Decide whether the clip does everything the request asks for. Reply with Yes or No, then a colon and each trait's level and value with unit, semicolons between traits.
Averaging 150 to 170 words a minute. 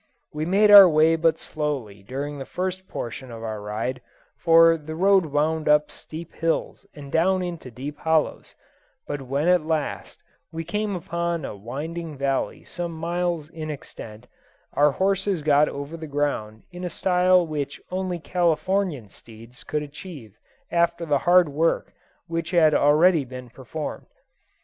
Yes: average, 155 wpm